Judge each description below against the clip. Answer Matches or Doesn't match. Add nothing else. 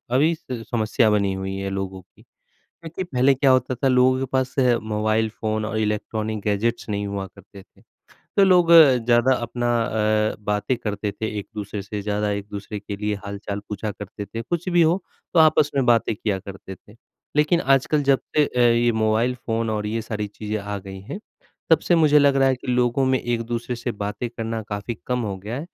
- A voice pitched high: Doesn't match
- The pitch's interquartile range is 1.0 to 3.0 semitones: Doesn't match